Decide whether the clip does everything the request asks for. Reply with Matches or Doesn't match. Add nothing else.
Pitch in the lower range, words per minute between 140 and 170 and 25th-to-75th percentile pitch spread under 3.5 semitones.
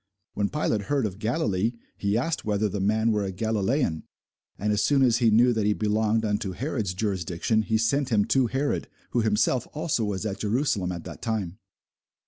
Doesn't match